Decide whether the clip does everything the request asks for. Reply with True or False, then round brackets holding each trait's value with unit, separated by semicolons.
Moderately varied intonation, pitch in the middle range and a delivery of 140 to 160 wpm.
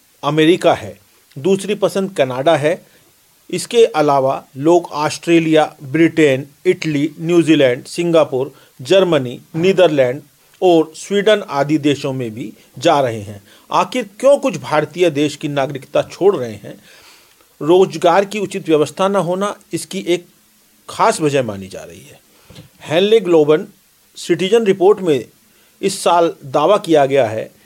False (4.6 semitones; 165 Hz; 130 wpm)